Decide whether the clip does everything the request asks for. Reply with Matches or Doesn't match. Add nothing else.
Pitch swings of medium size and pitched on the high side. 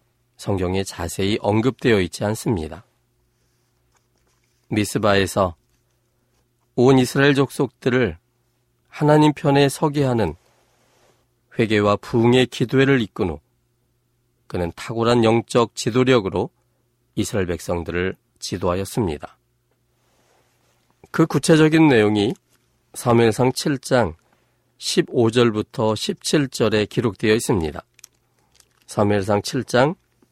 Doesn't match